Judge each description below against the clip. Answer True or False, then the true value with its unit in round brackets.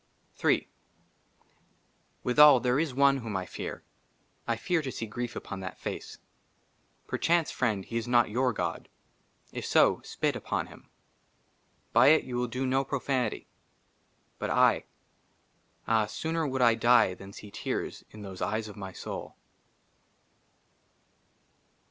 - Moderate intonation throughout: True (3.8 semitones)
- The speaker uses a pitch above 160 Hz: False (120 Hz)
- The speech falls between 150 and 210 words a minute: False (140 wpm)